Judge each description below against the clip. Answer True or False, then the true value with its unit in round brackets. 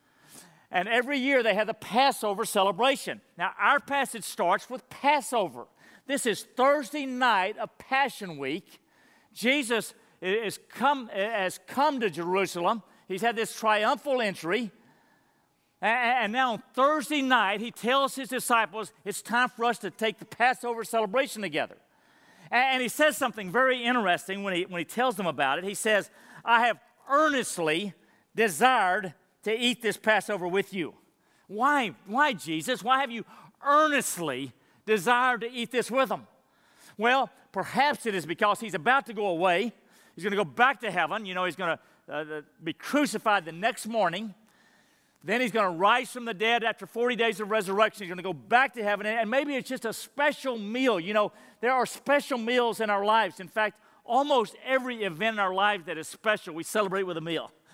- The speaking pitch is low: False (225 Hz)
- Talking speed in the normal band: True (175 wpm)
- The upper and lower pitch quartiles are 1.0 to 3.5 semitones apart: False (4.6 semitones)